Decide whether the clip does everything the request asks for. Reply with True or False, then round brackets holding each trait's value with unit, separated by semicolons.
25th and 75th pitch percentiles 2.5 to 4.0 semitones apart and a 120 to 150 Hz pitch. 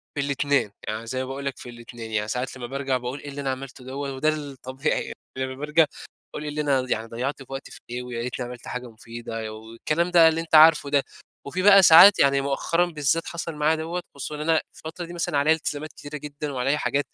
True (3.6 semitones; 140 Hz)